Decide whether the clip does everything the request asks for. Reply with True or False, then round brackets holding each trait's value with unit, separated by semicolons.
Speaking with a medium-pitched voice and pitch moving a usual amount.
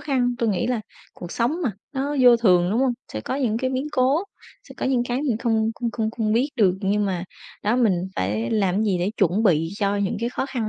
False (225 Hz; 4.3 semitones)